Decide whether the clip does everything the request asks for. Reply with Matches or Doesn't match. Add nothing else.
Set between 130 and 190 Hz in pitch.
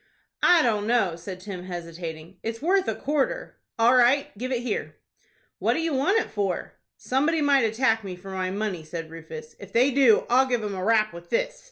Doesn't match